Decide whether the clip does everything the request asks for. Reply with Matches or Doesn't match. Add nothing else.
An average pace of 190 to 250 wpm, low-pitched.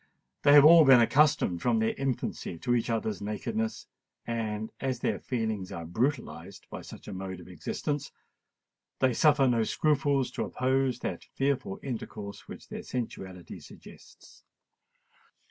Doesn't match